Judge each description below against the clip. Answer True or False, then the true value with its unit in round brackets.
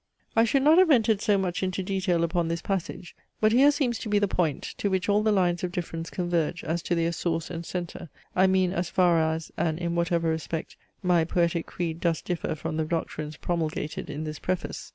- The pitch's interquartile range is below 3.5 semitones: True (2.6 semitones)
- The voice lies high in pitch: False (175 Hz)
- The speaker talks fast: True (215 wpm)